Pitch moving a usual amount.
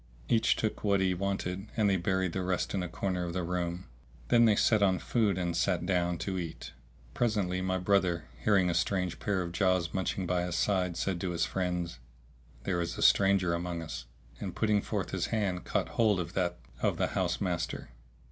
No: narrow, 2.1 semitones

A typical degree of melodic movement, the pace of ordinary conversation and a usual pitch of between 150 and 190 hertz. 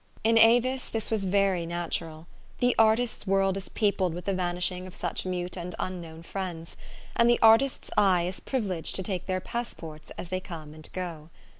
Yes: average, 4.0 semitones; average, 185 wpm; medium, 185 Hz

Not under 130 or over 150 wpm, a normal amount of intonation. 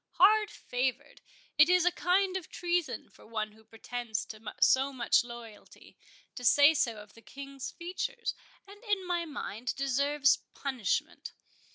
No: average, 145 wpm; wide, 6.9 semitones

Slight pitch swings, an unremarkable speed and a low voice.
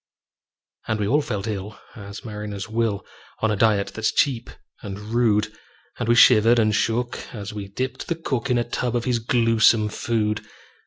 Yes: narrow, 2.1 semitones; average, 175 wpm; low, 110 Hz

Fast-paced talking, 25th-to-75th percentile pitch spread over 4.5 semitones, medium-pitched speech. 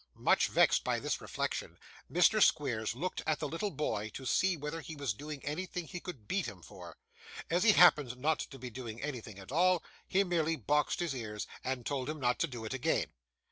Yes: fast, 210 wpm; wide, 5.4 semitones; medium, 150 Hz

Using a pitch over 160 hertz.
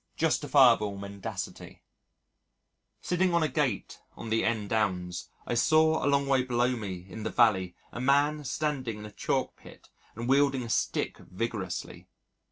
No: low, 120 Hz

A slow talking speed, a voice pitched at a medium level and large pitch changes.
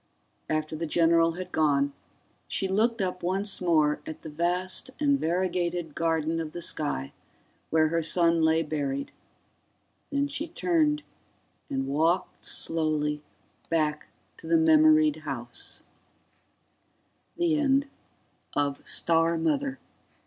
No: slow, 105 wpm; medium, 165 Hz; average, 2.8 semitones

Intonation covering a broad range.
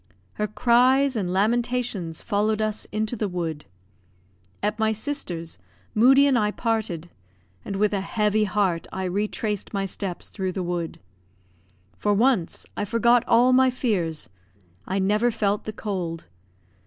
No: average, 3.5 semitones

